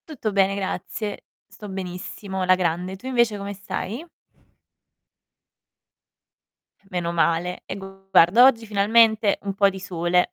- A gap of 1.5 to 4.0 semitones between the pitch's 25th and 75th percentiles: Yes, narrow, 2.5 semitones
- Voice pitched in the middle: No, high, 195 Hz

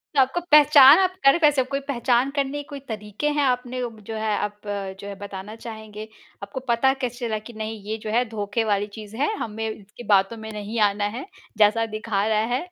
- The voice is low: No, high, 220 Hz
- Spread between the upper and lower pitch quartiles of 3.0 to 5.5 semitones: Yes, average, 3.6 semitones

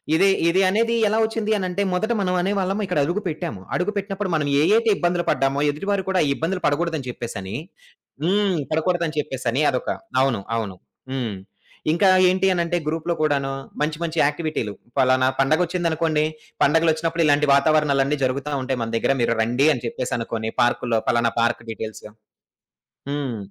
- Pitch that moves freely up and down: Yes, wide, 5.7 semitones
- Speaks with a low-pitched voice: No, medium, 155 Hz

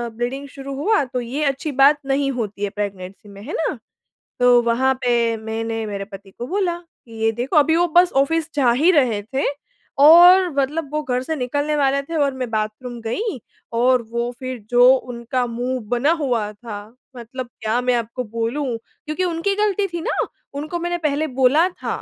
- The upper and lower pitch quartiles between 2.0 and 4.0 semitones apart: No, average, 4.6 semitones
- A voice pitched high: Yes, very high, 255 Hz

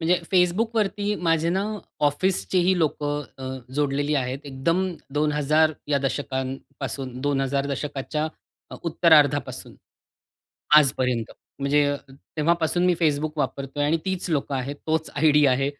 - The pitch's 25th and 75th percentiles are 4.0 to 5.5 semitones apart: No, average, 3.0 semitones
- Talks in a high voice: No, medium, 145 Hz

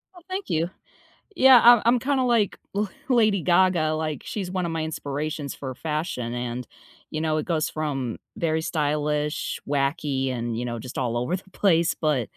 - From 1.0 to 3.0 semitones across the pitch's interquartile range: No, average, 5.2 semitones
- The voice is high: No, medium, 155 Hz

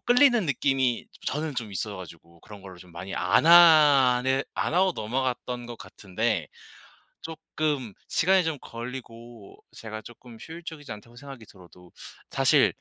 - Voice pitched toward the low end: Yes, low, 125 Hz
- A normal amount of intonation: No, wide, 6.1 semitones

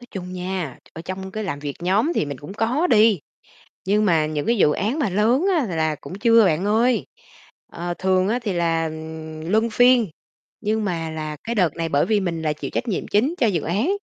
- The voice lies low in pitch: No, high, 190 Hz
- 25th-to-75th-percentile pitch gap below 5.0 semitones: No, wide, 5.4 semitones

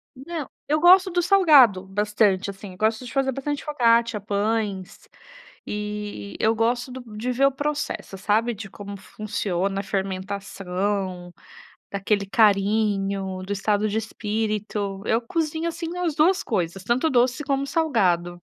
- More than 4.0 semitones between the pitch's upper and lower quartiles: Yes, average, 5.0 semitones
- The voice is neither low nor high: No, high, 215 Hz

